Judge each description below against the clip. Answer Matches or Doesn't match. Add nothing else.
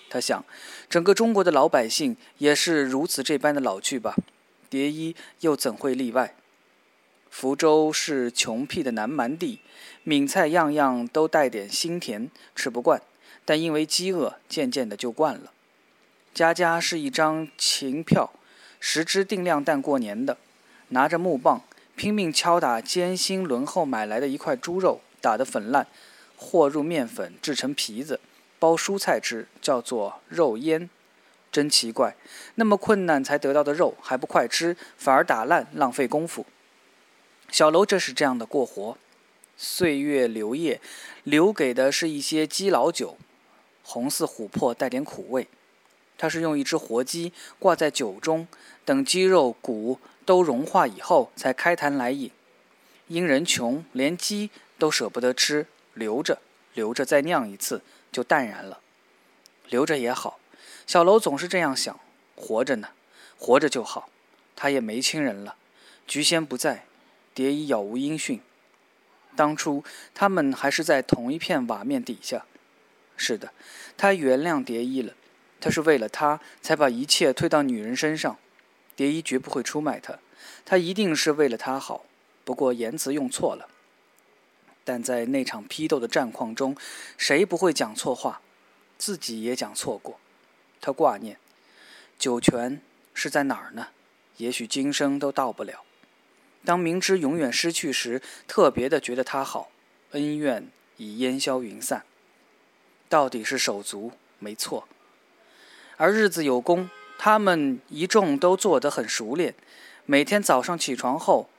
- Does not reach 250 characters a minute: Matches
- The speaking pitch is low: Doesn't match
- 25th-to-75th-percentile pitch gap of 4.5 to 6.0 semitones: Matches